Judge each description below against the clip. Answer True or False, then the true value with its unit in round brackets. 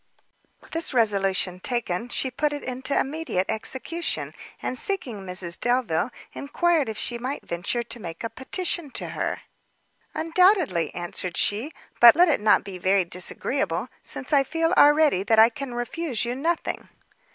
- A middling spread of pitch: False (7.0 semitones)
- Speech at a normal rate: True (150 wpm)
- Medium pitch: False (245 Hz)